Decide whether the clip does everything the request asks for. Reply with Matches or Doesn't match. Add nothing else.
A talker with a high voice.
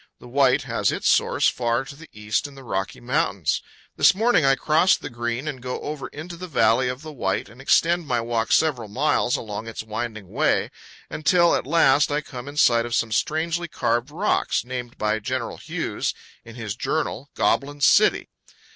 Doesn't match